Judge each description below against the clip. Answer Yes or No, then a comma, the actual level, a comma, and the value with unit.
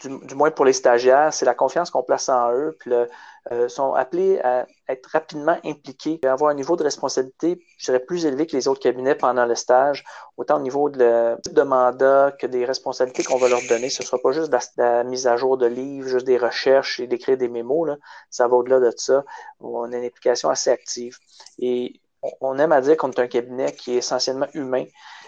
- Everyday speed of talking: No, fast, 235 wpm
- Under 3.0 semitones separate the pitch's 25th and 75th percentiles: No, average, 3.4 semitones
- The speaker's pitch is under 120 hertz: No, low, 130 Hz